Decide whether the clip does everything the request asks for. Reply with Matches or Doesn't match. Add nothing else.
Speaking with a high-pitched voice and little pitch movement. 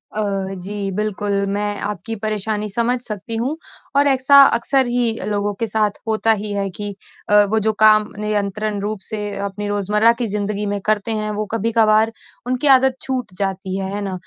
Matches